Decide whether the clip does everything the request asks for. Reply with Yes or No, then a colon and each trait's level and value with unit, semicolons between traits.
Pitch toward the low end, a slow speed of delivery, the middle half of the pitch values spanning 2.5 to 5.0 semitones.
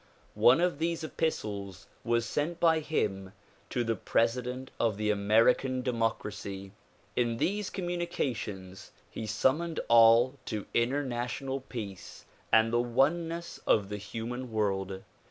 Yes: low, 120 Hz; slow, 130 wpm; average, 4.6 semitones